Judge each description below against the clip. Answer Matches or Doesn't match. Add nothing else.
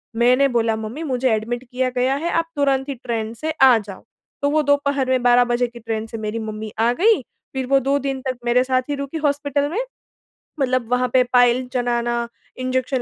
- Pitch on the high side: Matches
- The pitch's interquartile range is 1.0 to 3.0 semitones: Matches